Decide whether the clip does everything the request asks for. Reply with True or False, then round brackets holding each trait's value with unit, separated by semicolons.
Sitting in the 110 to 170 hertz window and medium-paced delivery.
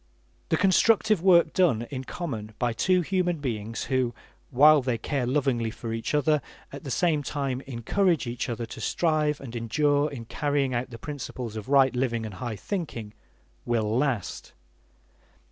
True (135 Hz; 160 wpm)